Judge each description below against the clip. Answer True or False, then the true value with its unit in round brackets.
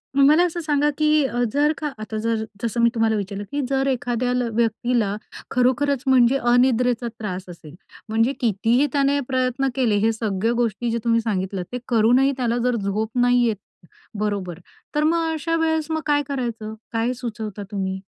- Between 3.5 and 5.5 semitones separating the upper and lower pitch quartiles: True (3.9 semitones)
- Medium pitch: False (240 Hz)